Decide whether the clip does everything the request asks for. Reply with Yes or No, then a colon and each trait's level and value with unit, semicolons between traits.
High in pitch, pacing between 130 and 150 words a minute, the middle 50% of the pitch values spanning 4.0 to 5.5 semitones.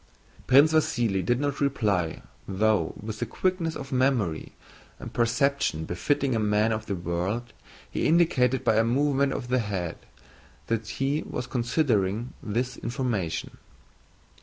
No: low, 120 Hz; slow, 135 wpm; average, 4.6 semitones